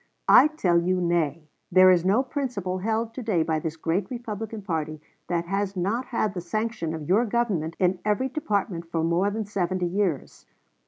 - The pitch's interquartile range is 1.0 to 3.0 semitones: No, average, 4.3 semitones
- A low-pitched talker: No, medium, 185 Hz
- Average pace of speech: Yes, average, 180 wpm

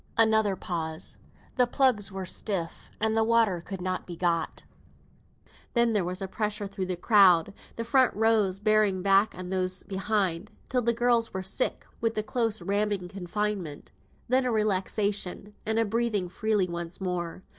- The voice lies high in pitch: Yes, high, 200 Hz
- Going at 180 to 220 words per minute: No, average, 160 wpm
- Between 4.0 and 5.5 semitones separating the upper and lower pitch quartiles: No, average, 3.2 semitones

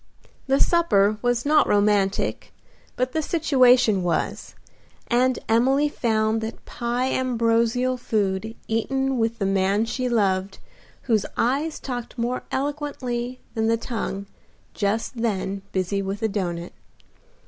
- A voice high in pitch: Yes, high, 230 Hz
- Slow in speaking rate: Yes, slow, 125 wpm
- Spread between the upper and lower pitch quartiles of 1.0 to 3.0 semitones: No, average, 3.9 semitones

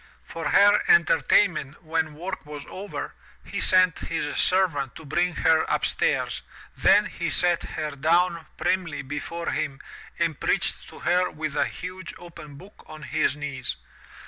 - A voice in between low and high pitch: Yes, medium, 160 Hz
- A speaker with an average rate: Yes, average, 150 wpm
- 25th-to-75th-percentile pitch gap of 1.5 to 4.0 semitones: Yes, average, 3.3 semitones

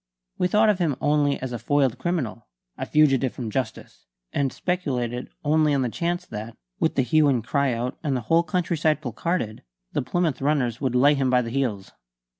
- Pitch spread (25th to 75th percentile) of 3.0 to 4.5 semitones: Yes, average, 4.0 semitones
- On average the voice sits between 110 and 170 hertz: Yes, medium, 140 Hz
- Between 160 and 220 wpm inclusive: Yes, average, 195 wpm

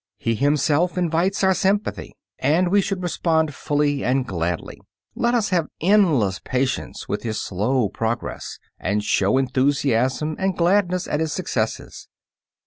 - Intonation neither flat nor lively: No, wide, 6.7 semitones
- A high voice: No, medium, 150 Hz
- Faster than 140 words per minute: No, slow, 135 wpm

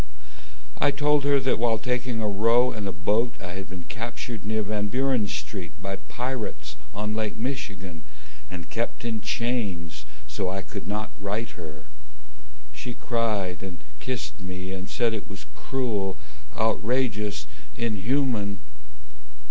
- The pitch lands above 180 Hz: No, low, 105 Hz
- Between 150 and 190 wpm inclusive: No, average, 140 wpm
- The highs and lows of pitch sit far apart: No, average, 3.9 semitones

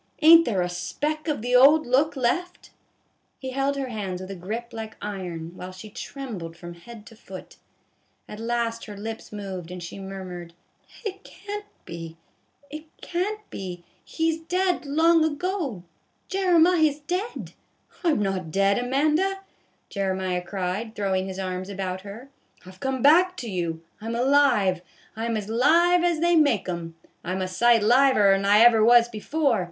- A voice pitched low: No, high, 230 Hz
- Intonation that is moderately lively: No, wide, 8.3 semitones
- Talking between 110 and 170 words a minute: No, average, 180 wpm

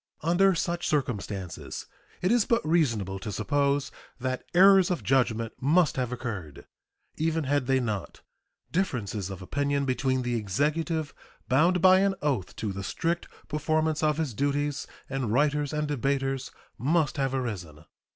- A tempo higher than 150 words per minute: No, average, 145 wpm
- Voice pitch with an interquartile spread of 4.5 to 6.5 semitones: Yes, average, 4.9 semitones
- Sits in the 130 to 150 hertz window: Yes, medium, 140 Hz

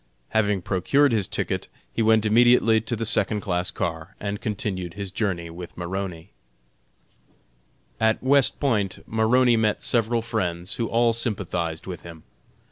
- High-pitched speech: No, low, 105 Hz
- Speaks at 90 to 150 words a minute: Yes, average, 140 wpm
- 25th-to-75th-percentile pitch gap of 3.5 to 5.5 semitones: Yes, average, 4.1 semitones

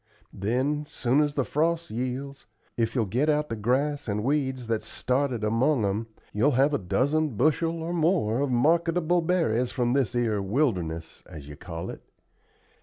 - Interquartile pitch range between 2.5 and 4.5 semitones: No, average, 5.1 semitones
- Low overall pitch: Yes, low, 130 Hz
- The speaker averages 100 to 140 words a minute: No, average, 170 wpm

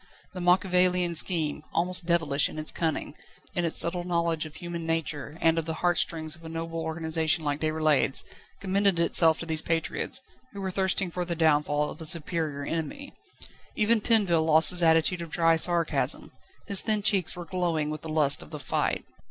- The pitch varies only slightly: Yes, narrow, 2.1 semitones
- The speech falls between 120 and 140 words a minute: No, average, 185 wpm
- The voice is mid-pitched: Yes, medium, 165 Hz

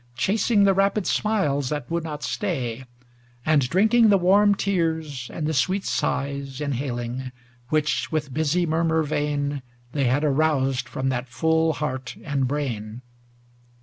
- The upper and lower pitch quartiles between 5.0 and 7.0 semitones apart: No, average, 4.1 semitones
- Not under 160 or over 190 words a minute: No, average, 140 wpm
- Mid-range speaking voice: Yes, medium, 150 Hz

